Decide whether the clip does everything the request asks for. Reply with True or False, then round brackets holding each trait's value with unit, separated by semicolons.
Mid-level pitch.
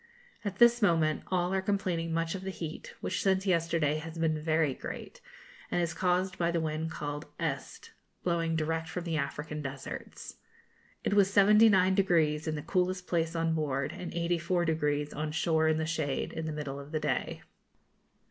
True (165 Hz)